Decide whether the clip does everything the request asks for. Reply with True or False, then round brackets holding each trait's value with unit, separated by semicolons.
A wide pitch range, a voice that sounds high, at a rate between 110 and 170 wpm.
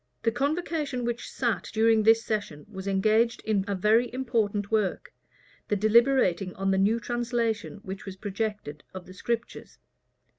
False (3.2 semitones; 220 Hz; 150 wpm)